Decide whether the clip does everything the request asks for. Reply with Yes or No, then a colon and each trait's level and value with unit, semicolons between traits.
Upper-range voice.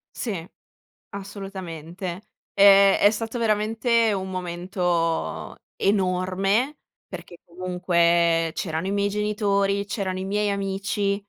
Yes: high, 195 Hz